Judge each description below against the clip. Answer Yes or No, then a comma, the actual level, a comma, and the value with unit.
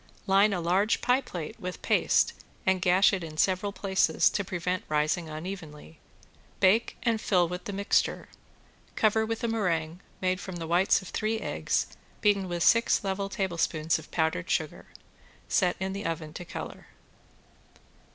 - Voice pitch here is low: No, medium, 185 Hz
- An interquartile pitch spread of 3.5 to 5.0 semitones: No, average, 3.1 semitones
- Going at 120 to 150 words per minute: No, average, 160 wpm